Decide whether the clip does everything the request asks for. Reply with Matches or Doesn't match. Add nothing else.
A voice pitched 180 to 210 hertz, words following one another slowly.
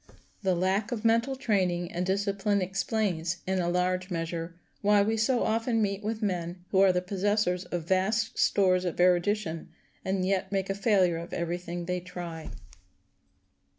Doesn't match